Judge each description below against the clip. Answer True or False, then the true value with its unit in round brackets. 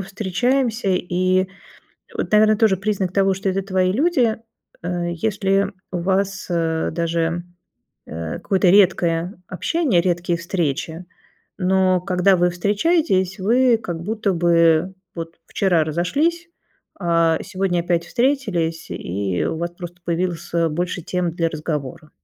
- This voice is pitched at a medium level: True (180 Hz)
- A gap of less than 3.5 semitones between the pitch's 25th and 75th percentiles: True (2.7 semitones)